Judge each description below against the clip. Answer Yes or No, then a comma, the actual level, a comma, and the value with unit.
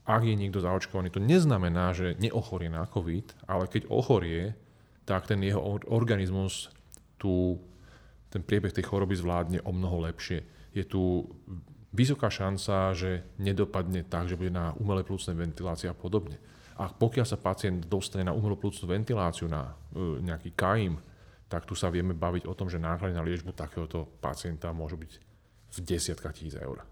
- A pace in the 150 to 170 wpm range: Yes, average, 160 wpm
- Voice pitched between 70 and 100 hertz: Yes, very low, 95 Hz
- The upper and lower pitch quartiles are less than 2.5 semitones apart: No, average, 2.8 semitones